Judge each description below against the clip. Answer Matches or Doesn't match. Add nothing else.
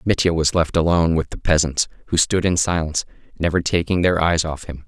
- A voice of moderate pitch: Doesn't match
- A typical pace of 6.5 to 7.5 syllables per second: Doesn't match